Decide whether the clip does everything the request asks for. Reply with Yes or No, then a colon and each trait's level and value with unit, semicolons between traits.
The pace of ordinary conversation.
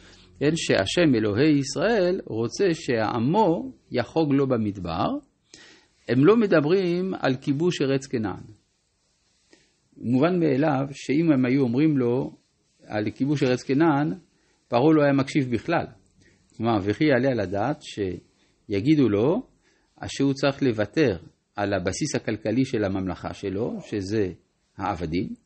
Yes: average, 120 wpm